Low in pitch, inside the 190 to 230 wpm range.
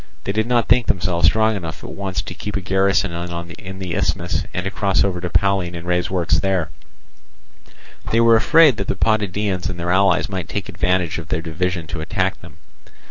Yes: very low, 95 Hz; average, 200 wpm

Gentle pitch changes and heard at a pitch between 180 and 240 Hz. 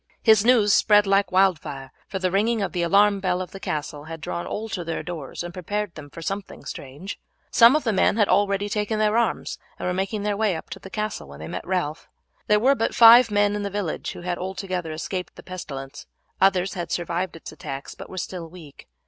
No: average, 3.5 semitones; high, 190 Hz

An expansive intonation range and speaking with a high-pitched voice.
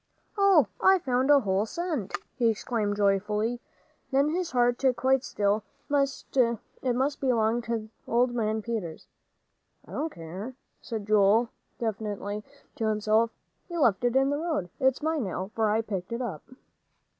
No: average, 4.1 semitones; high, 235 Hz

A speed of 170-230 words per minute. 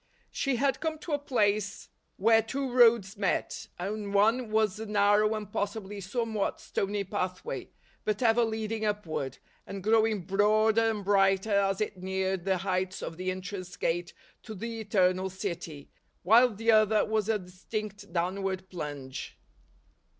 No: average, 150 wpm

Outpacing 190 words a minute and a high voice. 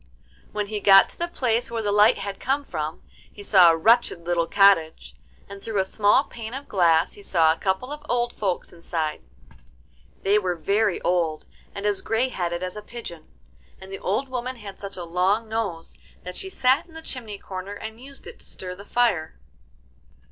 Yes: average, 200 wpm; high, 200 Hz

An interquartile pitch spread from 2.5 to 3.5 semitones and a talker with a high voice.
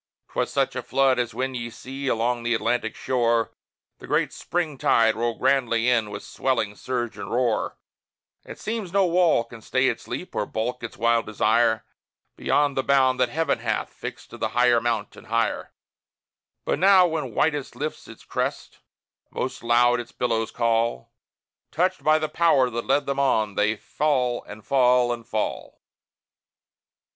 No: average, 3.0 semitones; low, 125 Hz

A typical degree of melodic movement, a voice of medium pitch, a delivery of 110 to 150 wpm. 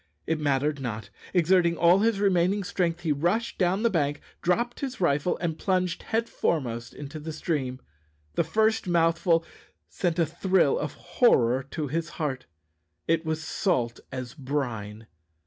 Yes: average, 4.5 semitones; medium, 165 Hz; average, 145 wpm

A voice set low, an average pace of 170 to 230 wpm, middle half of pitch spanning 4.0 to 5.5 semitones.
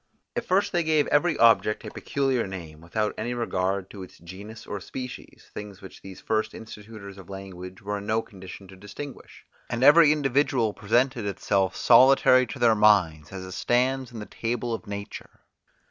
Yes: low, 110 Hz; average, 175 wpm; average, 4.7 semitones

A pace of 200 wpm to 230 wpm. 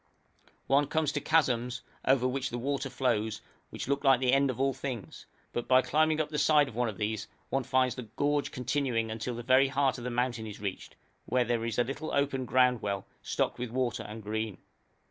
Yes: fast, 205 wpm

